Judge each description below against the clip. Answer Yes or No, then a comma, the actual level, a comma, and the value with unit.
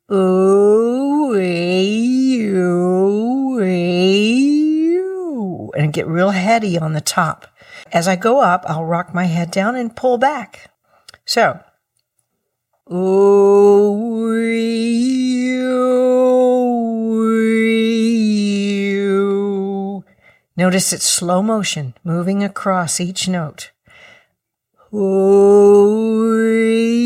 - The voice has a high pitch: Yes, high, 205 Hz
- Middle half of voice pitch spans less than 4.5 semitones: Yes, average, 3.7 semitones